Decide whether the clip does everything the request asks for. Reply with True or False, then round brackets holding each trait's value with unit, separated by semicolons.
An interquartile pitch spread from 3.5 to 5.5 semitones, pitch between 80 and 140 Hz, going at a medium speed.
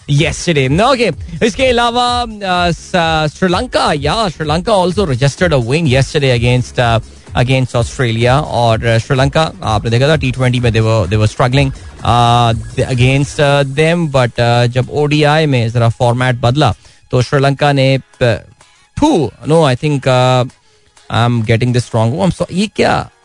True (4.7 semitones; 135 Hz; 155 wpm)